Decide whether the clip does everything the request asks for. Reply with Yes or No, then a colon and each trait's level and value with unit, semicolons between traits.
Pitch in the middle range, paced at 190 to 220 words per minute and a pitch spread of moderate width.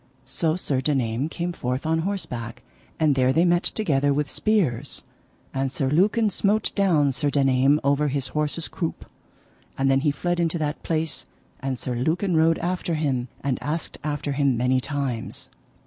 No: medium, 145 Hz; average, 165 wpm; average, 3.6 semitones